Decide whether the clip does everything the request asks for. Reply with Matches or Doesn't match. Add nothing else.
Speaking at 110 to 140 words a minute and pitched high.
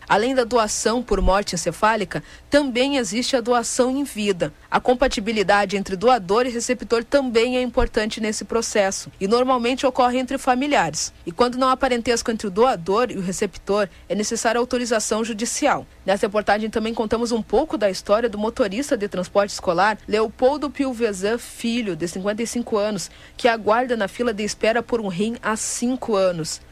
Doesn't match